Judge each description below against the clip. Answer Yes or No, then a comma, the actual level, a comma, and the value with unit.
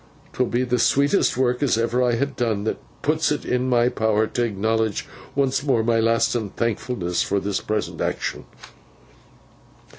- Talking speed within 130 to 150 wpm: No, average, 160 wpm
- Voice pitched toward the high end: No, low, 120 Hz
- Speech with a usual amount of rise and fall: No, narrow, 2.2 semitones